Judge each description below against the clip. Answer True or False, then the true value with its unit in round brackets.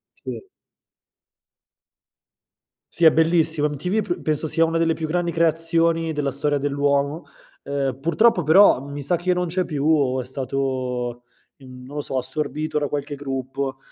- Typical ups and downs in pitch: True (3.2 semitones)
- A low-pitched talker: False (150 Hz)